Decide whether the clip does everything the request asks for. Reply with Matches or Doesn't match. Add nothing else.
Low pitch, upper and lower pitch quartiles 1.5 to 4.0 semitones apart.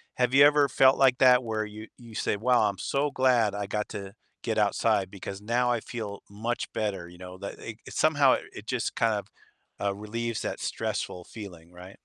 Matches